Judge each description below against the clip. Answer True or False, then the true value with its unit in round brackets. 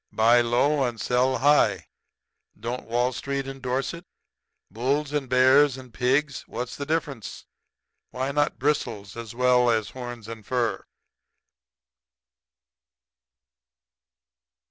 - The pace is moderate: False (110 wpm)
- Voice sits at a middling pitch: False (125 Hz)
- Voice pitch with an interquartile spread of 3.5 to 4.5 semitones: False (2.6 semitones)